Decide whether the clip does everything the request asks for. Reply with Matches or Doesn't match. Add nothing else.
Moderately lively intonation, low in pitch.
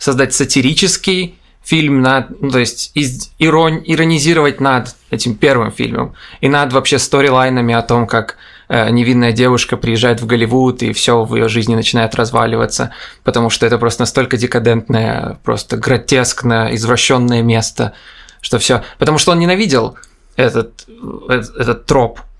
Matches